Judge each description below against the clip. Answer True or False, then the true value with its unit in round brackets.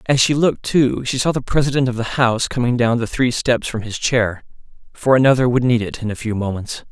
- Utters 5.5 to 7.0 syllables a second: True (5.7 syllables/s)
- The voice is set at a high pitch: False (120 Hz)